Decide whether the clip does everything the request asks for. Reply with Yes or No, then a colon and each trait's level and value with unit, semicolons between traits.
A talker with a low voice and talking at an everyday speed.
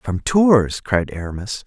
Yes: low, 110 Hz; average, 145 wpm